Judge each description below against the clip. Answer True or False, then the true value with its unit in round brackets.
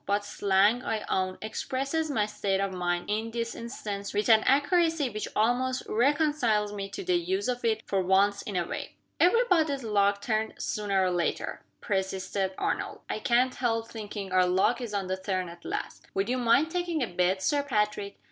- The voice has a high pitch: True (215 Hz)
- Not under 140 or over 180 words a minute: False (190 wpm)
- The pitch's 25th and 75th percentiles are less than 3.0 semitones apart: False (4.7 semitones)